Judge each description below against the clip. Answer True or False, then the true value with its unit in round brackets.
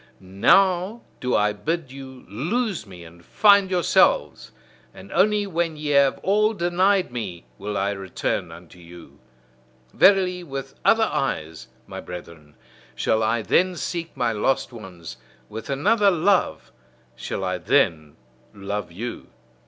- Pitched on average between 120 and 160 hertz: True (135 Hz)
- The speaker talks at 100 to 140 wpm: True (135 wpm)